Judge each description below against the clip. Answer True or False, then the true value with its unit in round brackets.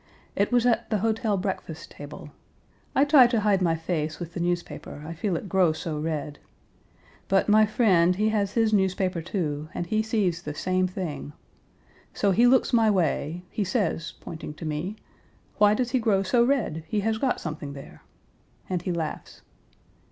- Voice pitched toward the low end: False (185 Hz)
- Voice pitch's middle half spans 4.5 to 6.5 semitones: True (4.8 semitones)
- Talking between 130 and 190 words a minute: True (180 wpm)